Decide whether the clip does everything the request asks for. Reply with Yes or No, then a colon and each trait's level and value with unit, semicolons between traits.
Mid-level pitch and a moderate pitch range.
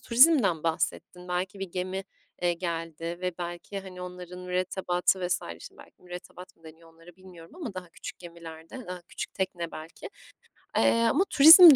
No: medium, 180 Hz; narrow, 2.0 semitones